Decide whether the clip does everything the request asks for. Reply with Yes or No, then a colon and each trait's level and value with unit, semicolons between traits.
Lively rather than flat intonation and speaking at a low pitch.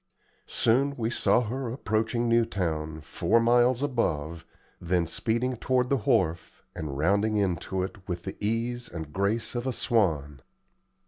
Yes: wide, 6.0 semitones; low, 110 Hz